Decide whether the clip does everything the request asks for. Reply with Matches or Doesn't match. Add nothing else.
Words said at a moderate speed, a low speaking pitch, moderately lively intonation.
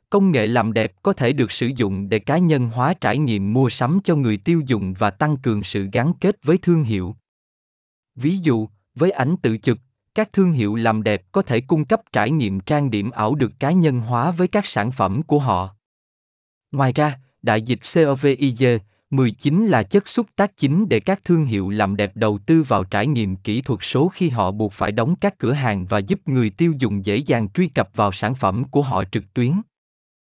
Doesn't match